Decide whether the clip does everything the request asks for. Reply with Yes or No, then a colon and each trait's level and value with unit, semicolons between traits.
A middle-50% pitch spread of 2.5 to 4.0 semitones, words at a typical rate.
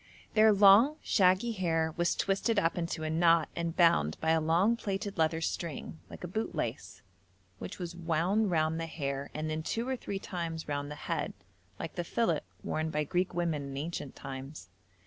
Yes: average, 3.5 semitones; average, 185 wpm